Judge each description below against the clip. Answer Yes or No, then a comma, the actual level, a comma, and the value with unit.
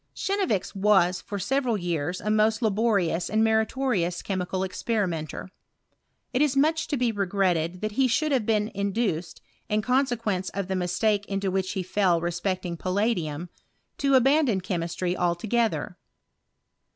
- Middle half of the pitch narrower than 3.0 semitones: No, average, 4.2 semitones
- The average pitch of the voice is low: No, high, 200 Hz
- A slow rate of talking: No, average, 145 wpm